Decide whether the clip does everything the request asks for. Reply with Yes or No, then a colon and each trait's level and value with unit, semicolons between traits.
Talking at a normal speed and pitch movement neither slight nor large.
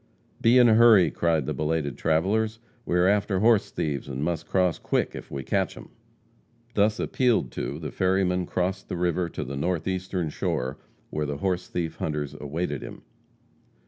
Yes: average, 175 wpm; average, 4.2 semitones